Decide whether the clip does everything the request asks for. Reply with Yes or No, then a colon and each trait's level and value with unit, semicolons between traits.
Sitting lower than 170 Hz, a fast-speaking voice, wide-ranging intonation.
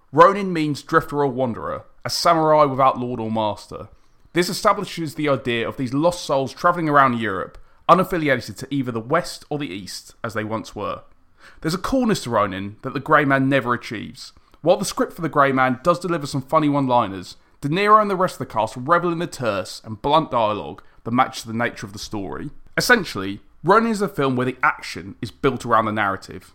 Yes: medium, 140 Hz; fast, 210 wpm; wide, 5.7 semitones